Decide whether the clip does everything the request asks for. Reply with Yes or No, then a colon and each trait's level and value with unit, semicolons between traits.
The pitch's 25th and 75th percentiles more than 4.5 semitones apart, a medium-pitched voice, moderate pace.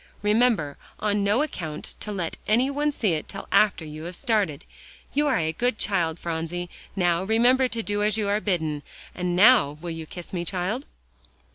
No: average, 5.1 semitones; high, 195 Hz; average, 185 wpm